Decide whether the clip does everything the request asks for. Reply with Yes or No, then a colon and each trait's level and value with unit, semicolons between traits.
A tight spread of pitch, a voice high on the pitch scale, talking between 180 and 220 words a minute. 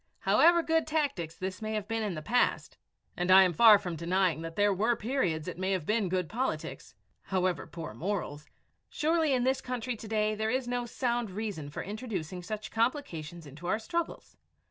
No: wide, 5.4 semitones; high, 210 Hz; average, 190 wpm